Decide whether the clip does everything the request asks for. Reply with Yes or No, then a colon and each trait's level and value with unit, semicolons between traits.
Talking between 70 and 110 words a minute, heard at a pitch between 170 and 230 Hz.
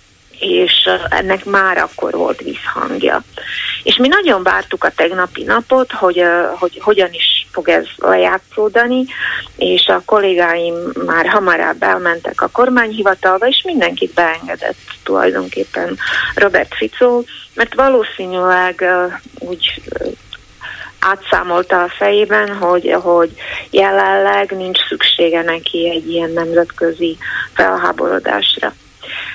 Yes: slow, 105 wpm; medium, 185 Hz